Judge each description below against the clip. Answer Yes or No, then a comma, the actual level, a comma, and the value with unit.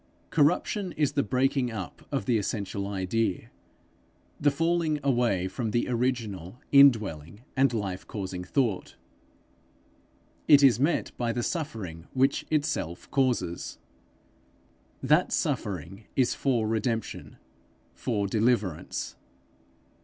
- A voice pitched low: Yes, low, 120 Hz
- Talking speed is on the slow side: Yes, slow, 110 wpm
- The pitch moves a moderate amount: No, wide, 5.8 semitones